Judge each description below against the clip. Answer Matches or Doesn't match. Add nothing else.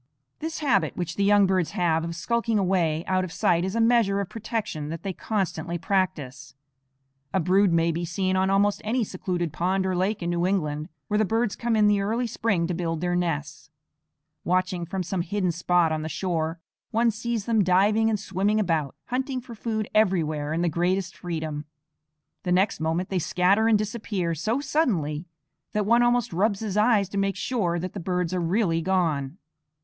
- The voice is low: Doesn't match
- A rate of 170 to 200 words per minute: Matches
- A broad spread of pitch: Doesn't match